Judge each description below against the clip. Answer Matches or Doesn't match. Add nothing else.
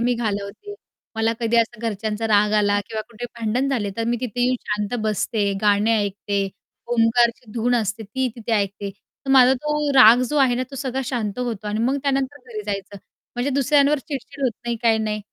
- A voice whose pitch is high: Matches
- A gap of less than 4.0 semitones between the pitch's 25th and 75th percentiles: Matches